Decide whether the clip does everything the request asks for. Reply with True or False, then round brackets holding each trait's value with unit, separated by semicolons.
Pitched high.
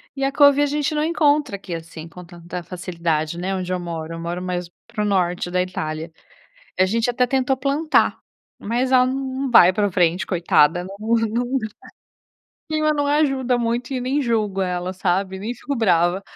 True (200 Hz)